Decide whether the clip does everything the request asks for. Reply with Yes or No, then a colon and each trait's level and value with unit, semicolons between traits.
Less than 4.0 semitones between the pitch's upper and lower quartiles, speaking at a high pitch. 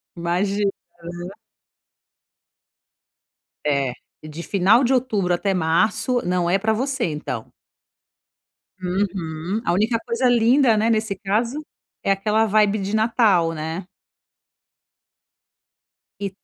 No: average, 4.3 semitones; high, 200 Hz